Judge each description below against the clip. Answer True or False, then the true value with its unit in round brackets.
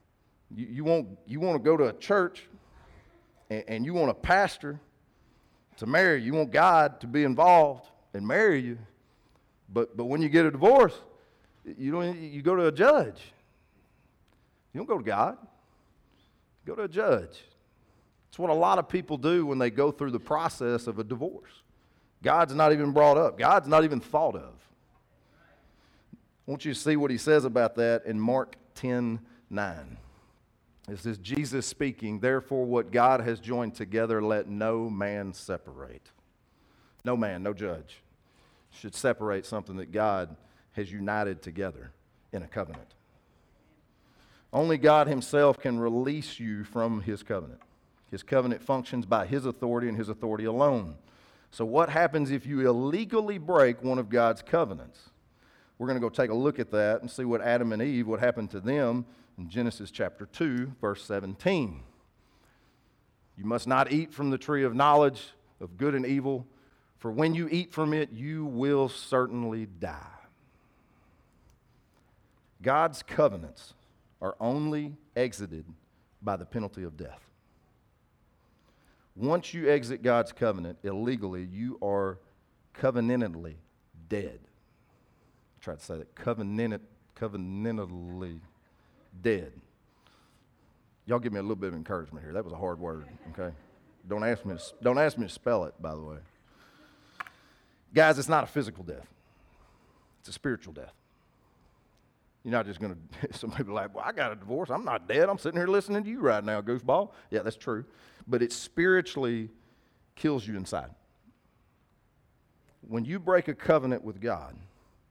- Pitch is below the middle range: True (120 Hz)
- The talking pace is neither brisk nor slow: True (160 wpm)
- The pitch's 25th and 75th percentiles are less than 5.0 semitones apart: False (5.5 semitones)